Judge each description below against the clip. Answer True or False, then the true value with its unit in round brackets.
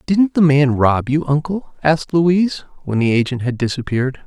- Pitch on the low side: False (145 Hz)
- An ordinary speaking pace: True (185 wpm)